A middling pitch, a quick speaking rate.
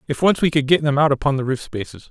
Yes: medium, 145 Hz; fast, 315 wpm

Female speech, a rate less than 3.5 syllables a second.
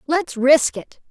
Yes: female; 3.3 syllables/s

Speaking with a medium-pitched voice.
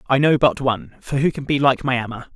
No: low, 130 Hz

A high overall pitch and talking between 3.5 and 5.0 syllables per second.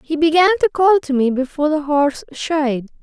No: very high, 300 Hz; 5.3 syllables/s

